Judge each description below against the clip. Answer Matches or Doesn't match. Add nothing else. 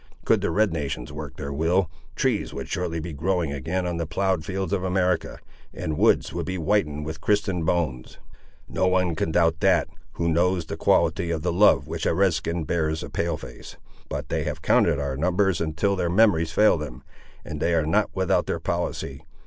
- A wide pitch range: Doesn't match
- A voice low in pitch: Matches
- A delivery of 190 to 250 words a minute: Matches